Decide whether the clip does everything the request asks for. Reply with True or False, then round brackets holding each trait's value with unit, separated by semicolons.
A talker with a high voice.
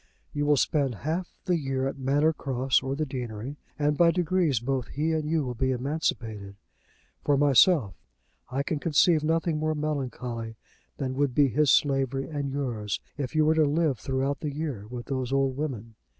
False (140 Hz)